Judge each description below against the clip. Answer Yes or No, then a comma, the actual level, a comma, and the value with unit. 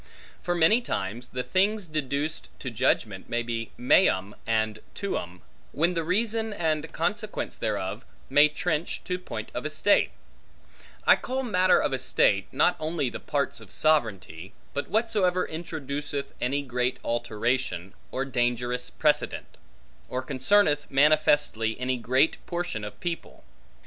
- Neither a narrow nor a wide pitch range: No, wide, 6.4 semitones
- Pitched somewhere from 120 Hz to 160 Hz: Yes, medium, 140 Hz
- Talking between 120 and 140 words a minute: Yes, slow, 135 wpm